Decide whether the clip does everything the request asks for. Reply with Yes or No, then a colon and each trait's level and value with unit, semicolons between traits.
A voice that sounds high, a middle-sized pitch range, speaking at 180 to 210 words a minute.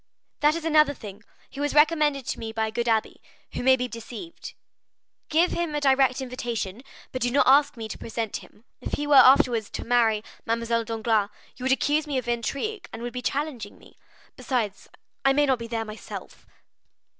Yes: very high, 250 Hz; average, 4.1 semitones; average, 190 wpm